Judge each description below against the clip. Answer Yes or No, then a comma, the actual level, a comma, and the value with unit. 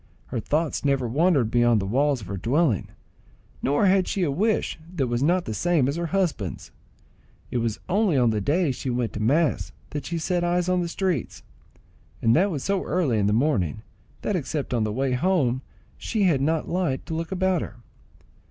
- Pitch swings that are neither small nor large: No, wide, 6.6 semitones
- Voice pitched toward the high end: No, medium, 145 Hz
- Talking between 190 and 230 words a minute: Yes, average, 200 wpm